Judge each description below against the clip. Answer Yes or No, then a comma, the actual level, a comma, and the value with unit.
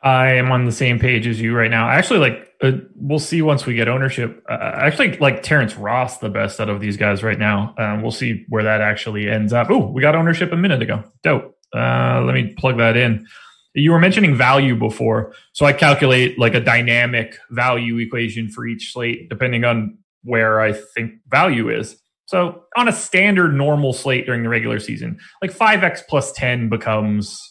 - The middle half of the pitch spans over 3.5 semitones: Yes, average, 4.1 semitones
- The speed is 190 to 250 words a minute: Yes, average, 200 wpm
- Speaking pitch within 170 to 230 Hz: No, low, 120 Hz